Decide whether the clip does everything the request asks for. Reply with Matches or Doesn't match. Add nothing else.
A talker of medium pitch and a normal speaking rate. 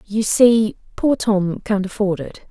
Doesn't match